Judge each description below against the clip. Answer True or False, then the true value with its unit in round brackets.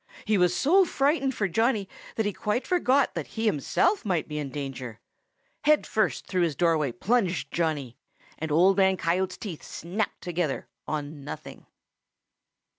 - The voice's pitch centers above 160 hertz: True (185 Hz)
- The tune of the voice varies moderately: False (6.4 semitones)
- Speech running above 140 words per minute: True (155 wpm)